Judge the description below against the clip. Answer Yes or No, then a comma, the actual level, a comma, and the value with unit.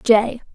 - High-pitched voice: Yes, high, 230 Hz